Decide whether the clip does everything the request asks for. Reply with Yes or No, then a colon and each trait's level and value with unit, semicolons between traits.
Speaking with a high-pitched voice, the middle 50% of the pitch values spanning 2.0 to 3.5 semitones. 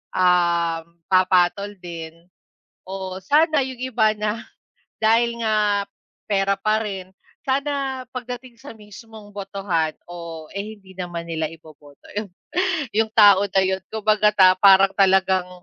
Yes: high, 200 Hz; average, 3.2 semitones